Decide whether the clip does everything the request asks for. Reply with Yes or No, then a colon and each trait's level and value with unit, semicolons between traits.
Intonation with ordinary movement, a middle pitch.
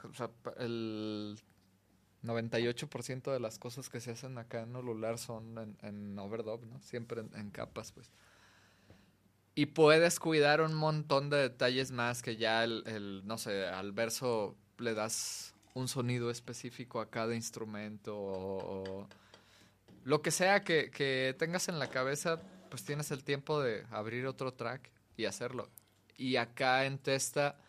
No: average, 3.9 semitones; low, 120 Hz